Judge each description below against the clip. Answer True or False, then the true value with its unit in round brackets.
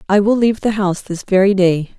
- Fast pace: True (240 wpm)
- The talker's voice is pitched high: True (200 Hz)